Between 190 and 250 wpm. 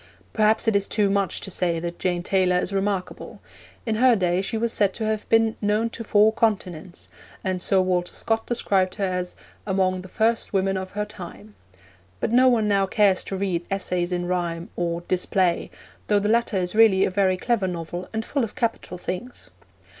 Yes: average, 195 wpm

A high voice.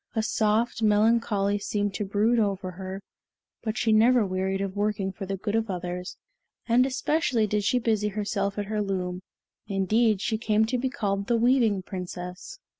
Yes: high, 210 Hz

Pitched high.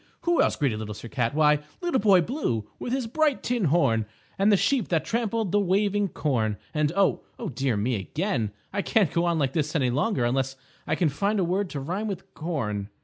No: medium, 165 Hz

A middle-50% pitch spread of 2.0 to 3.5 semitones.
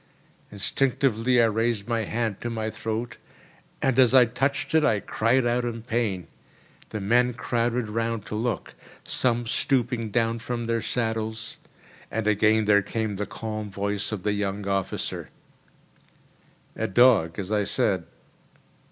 Yes: narrow, 2.4 semitones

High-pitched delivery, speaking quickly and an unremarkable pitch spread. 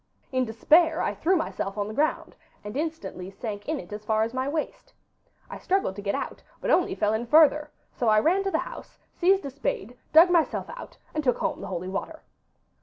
No: very high, 260 Hz; fast, 215 wpm; wide, 7.1 semitones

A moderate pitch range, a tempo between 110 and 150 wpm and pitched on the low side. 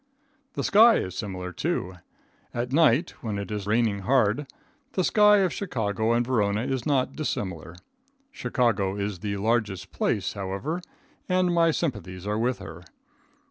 No: wide, 6.5 semitones; average, 145 wpm; low, 115 Hz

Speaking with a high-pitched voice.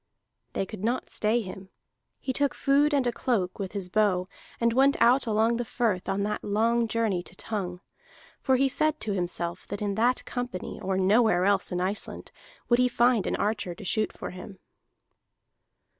Yes: high, 215 Hz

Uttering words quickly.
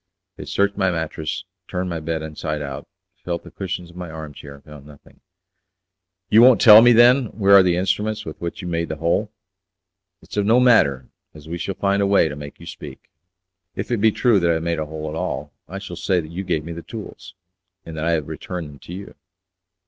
Yes: fast, 230 wpm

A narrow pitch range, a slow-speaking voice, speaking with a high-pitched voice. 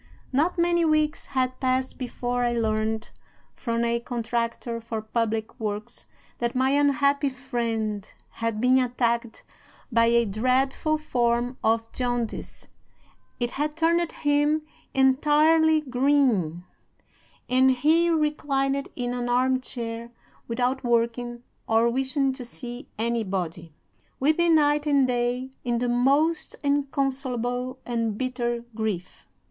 No: average, 3.1 semitones; slow, 120 wpm; very high, 250 Hz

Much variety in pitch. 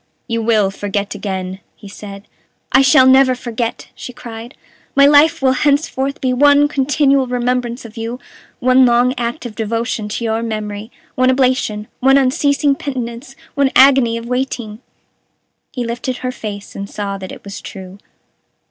No: average, 3.6 semitones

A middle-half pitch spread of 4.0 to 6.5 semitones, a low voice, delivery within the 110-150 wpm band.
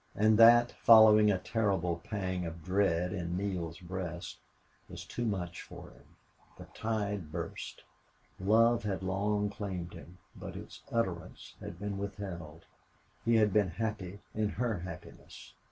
No: average, 3.4 semitones; low, 100 Hz; average, 140 wpm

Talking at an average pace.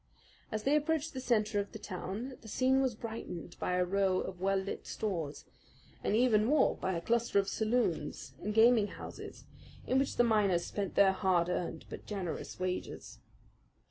Yes: average, 175 wpm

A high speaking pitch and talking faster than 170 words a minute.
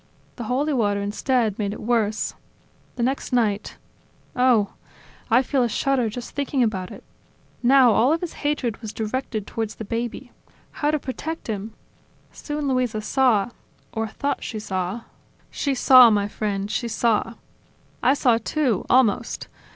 No: high, 235 Hz; average, 160 wpm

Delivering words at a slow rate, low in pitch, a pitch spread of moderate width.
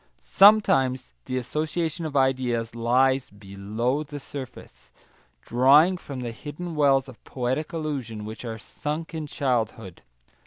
Yes: slow, 125 wpm; low, 130 Hz; average, 4.3 semitones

